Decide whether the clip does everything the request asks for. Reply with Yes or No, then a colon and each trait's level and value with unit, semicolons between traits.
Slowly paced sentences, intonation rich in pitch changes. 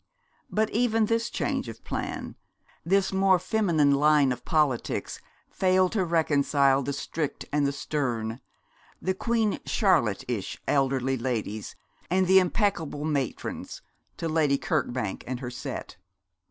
Yes: slow, 130 wpm; wide, 6.0 semitones